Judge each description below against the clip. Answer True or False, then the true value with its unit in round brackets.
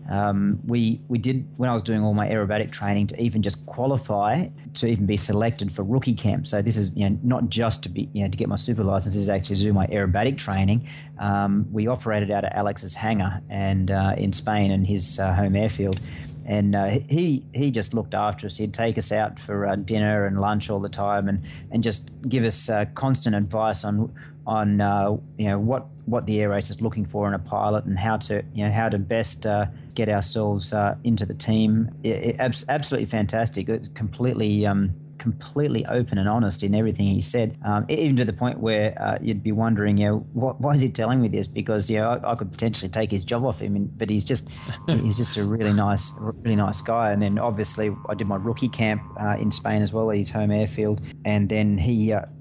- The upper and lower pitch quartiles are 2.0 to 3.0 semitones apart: True (2.4 semitones)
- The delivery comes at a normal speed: False (230 wpm)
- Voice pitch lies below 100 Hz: False (105 Hz)